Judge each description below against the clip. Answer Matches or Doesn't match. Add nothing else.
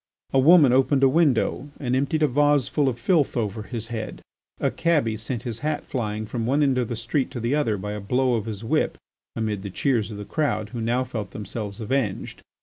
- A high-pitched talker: Doesn't match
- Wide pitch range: Doesn't match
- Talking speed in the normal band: Doesn't match